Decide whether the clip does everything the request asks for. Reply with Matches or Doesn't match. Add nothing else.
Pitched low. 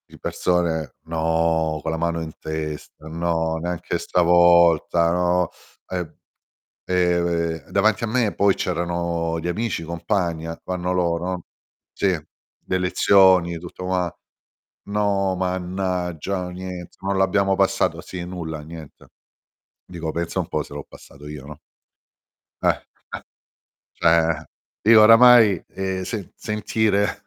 Matches